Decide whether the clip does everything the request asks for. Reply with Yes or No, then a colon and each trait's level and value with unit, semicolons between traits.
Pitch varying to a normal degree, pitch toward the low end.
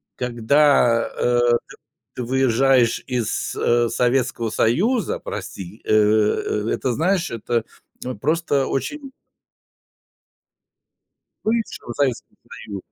Yes: average, 3.8 semitones; low, 125 Hz